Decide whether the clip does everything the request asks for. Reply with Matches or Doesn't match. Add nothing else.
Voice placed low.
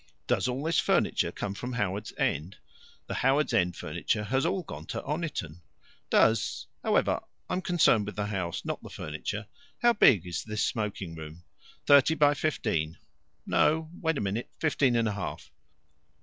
Matches